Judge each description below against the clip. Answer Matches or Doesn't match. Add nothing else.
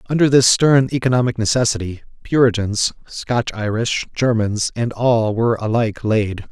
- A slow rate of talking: Matches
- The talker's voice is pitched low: Matches